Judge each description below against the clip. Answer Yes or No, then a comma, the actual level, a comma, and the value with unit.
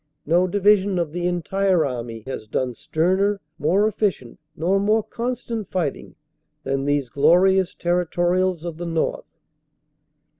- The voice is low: No, medium, 175 Hz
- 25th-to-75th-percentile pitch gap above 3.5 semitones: Yes, average, 4.1 semitones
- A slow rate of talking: Yes, slow, 125 wpm